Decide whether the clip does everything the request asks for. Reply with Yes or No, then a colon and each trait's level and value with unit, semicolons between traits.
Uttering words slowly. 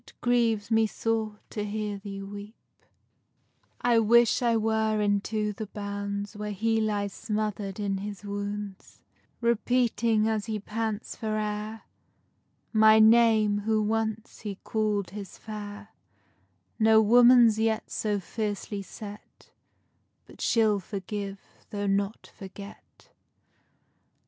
Yes: slow, 100 wpm